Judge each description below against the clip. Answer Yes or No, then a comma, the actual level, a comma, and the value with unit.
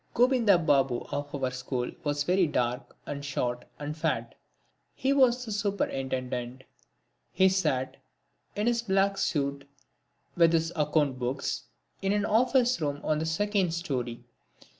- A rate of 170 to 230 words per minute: No, average, 140 wpm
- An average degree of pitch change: No, wide, 6.8 semitones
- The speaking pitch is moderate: Yes, medium, 155 Hz